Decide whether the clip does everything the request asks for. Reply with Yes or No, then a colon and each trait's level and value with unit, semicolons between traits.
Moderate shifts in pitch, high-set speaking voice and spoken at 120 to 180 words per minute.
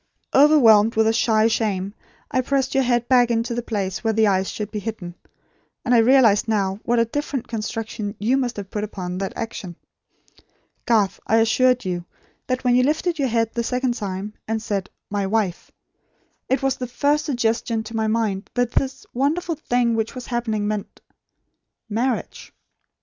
Yes: average, 3.0 semitones; high, 225 Hz; average, 175 wpm